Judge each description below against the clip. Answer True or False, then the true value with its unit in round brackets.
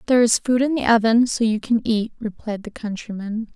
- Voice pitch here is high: True (225 Hz)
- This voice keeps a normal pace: False (220 wpm)